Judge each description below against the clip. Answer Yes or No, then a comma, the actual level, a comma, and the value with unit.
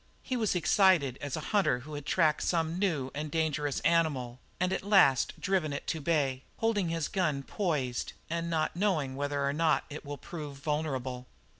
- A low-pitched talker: No, medium, 155 Hz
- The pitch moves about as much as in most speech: Yes, average, 3.6 semitones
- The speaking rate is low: No, average, 180 wpm